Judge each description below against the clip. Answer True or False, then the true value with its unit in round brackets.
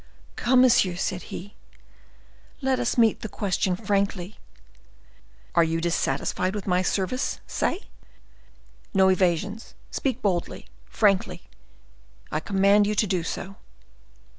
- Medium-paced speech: False (115 wpm)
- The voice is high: True (195 Hz)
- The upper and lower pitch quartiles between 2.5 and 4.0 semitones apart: True (3.2 semitones)